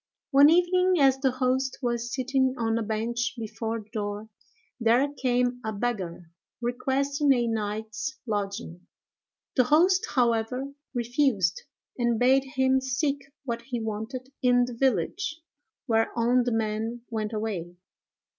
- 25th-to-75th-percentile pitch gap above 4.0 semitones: No, average, 3.1 semitones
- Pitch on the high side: Yes, high, 240 Hz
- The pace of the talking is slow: Yes, slow, 130 wpm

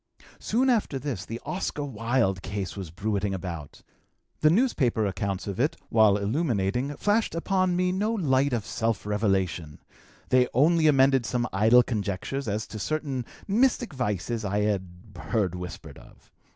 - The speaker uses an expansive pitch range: Yes, wide, 6.7 semitones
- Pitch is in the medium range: No, low, 115 Hz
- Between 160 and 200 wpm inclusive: No, average, 150 wpm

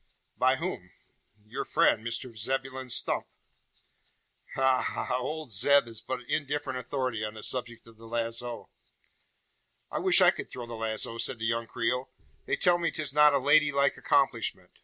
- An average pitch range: Yes, average, 3.3 semitones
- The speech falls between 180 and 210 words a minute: No, average, 165 wpm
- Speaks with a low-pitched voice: Yes, low, 125 Hz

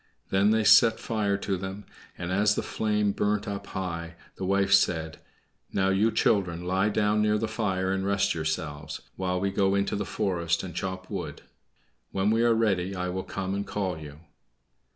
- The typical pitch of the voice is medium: No, very low, 95 Hz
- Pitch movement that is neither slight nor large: No, narrow, 2.3 semitones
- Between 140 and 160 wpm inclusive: No, average, 185 wpm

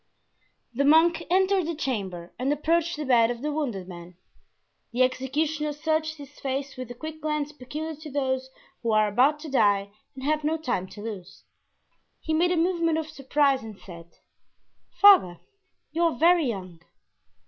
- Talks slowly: No, average, 170 wpm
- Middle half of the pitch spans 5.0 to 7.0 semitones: Yes, average, 5.3 semitones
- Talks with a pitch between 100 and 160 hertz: No, very high, 285 Hz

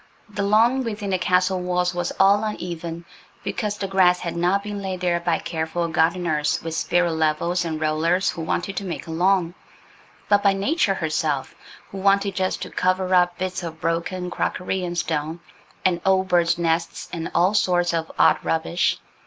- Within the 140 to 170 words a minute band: No, average, 180 wpm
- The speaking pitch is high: No, medium, 180 Hz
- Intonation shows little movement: Yes, narrow, 2.3 semitones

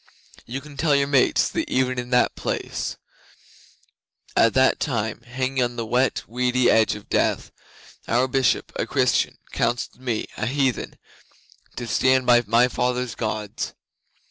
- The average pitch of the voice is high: No, low, 125 Hz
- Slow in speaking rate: No, average, 145 wpm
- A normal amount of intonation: No, narrow, 1.7 semitones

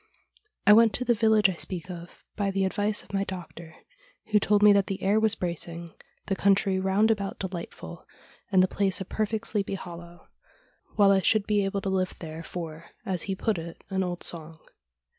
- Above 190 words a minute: Yes, average, 200 wpm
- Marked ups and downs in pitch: No, average, 2.7 semitones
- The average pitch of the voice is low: No, high, 195 Hz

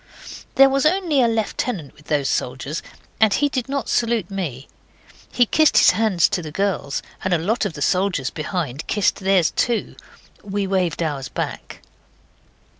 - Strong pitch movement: Yes, wide, 7.0 semitones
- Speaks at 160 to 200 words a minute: Yes, average, 165 wpm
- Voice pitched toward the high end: Yes, high, 195 Hz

